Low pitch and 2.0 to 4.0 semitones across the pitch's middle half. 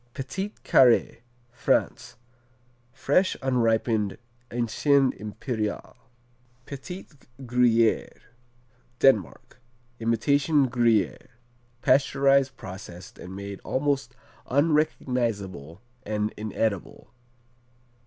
No: low, 120 Hz; average, 4.4 semitones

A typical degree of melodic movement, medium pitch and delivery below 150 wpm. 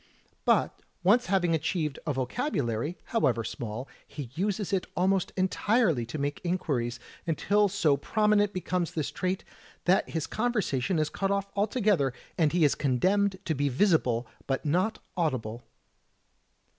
No: wide, 6.2 semitones; medium, 175 Hz; average, 140 wpm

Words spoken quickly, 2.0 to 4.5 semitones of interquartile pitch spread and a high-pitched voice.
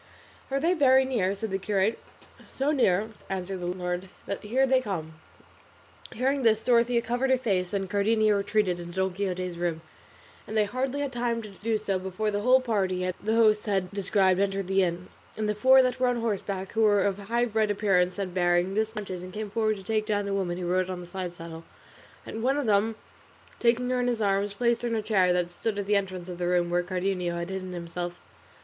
Yes: fast, 220 wpm; average, 3.7 semitones; high, 200 Hz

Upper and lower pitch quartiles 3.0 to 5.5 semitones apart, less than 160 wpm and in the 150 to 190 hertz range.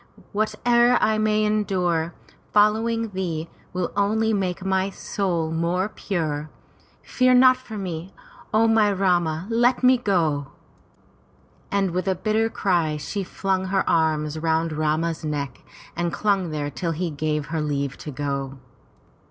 Yes: average, 5.0 semitones; average, 140 wpm; medium, 185 Hz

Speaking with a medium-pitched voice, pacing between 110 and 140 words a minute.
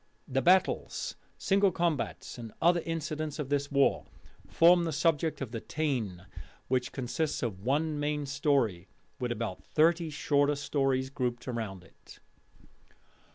Yes: medium, 145 Hz; slow, 135 wpm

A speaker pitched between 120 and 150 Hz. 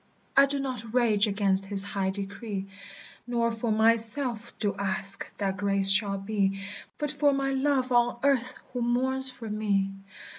No: high, 220 Hz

